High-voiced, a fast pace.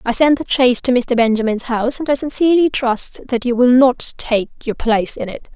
Yes: very high, 250 Hz; fast, 225 wpm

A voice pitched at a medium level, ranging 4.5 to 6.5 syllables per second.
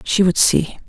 No: medium, 180 Hz; 4.2 syllables/s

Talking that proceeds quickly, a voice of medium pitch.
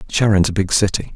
No: fast, 210 wpm; low, 100 Hz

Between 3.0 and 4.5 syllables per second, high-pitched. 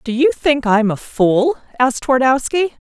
No: 5.0 syllables/s; very high, 260 Hz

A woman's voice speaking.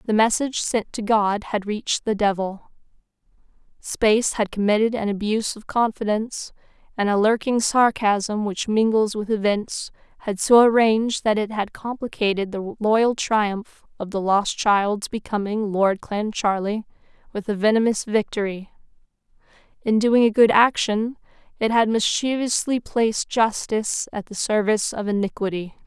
Yes: female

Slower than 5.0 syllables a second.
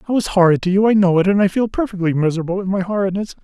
No: 7.4 syllables/s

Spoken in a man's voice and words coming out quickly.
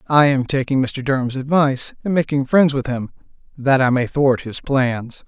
No: male; average, 195 wpm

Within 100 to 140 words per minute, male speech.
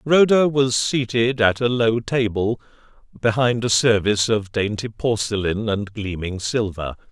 Yes: slow, 135 wpm; male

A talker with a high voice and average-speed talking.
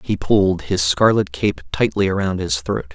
No: very low, 90 Hz; average, 185 wpm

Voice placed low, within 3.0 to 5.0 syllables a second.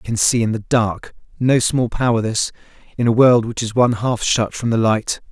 No: low, 115 Hz; 5.2 syllables/s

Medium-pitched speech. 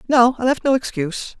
No: high, 245 Hz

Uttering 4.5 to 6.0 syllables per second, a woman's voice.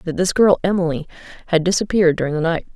No: 6.9 syllables/s; female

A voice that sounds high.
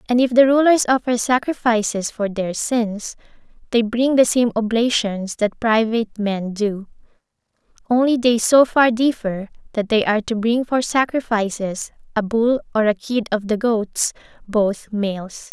Yes: high, 225 Hz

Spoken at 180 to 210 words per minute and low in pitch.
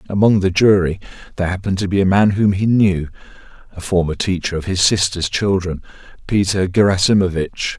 No: average, 160 wpm; very low, 95 Hz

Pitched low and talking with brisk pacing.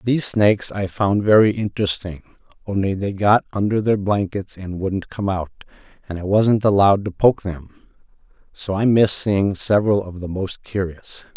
No: low, 100 Hz; average, 170 wpm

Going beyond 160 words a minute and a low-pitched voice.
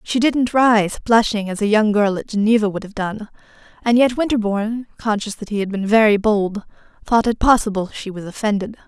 No: average, 195 wpm; high, 215 Hz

